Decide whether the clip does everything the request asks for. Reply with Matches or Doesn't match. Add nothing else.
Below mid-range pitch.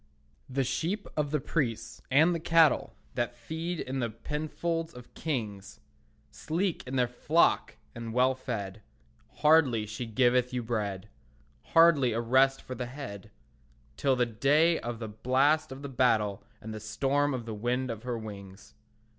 Matches